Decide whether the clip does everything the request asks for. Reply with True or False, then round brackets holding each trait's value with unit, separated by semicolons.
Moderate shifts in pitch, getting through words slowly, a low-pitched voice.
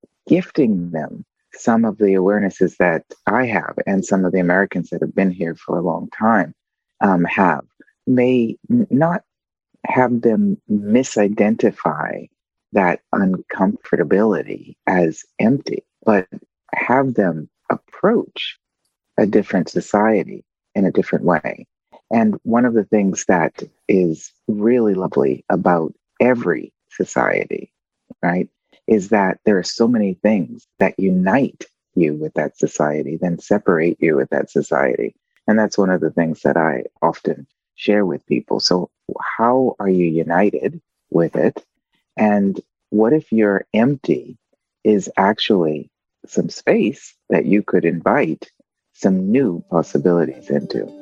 True (4.6 semitones; 130 wpm; 100 Hz)